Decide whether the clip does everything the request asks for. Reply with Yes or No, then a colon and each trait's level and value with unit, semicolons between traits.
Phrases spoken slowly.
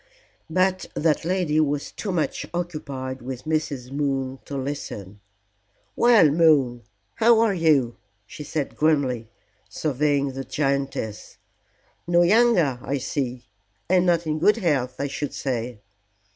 Yes: slow, 130 wpm